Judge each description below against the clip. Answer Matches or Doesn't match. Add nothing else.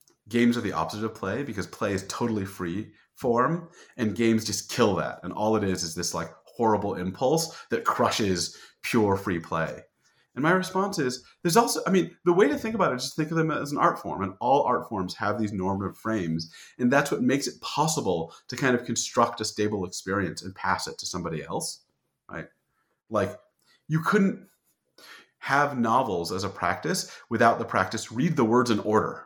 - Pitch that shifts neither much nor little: Doesn't match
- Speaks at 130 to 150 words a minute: Doesn't match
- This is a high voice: Doesn't match